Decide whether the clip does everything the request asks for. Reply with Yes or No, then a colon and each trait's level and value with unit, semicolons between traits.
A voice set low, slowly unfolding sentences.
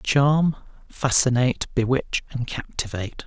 Yes: low, 130 Hz; slow, 90 wpm